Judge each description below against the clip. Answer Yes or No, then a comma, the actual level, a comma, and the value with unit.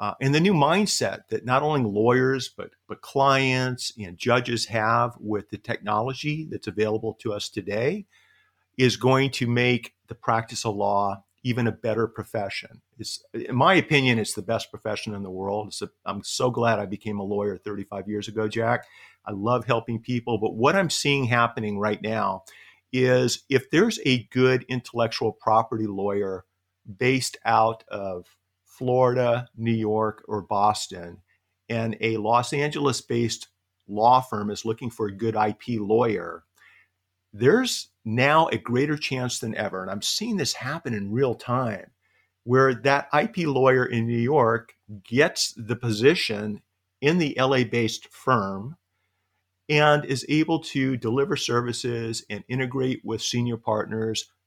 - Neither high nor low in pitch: No, low, 115 Hz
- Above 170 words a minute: No, average, 155 wpm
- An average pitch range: Yes, average, 3.6 semitones